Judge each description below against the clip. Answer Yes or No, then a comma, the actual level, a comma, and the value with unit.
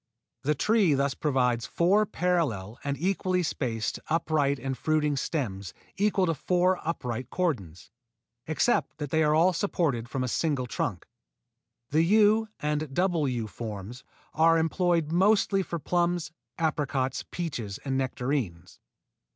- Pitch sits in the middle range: Yes, medium, 150 Hz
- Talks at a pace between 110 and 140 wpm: Yes, slow, 135 wpm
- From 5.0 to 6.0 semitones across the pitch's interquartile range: Yes, wide, 5.5 semitones